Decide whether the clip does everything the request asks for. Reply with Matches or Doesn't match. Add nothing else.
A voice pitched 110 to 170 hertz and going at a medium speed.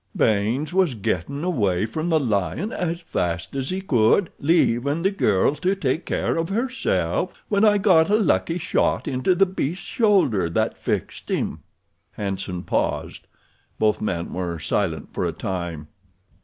Matches